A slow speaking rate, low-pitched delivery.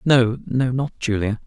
Yes: slow, 125 wpm; low, 120 Hz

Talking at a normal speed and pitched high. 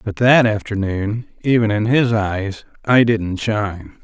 No: average, 150 wpm; low, 105 Hz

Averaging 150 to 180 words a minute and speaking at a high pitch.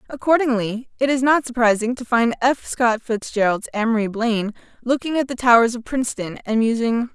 Yes: average, 170 wpm; high, 240 Hz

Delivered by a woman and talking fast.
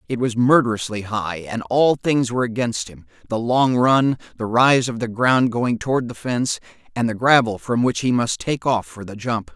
No: male; fast, 215 wpm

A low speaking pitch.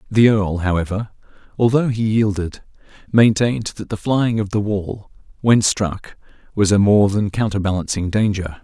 Yes: low, 105 Hz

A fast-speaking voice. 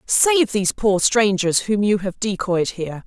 No: average, 175 wpm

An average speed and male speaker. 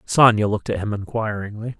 Yes: average, 165 wpm; male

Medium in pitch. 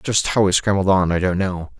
No: very low, 95 Hz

